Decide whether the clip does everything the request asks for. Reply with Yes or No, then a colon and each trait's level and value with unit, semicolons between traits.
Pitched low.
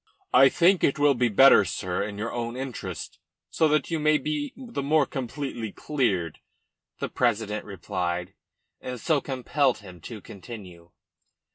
Yes: low, 120 Hz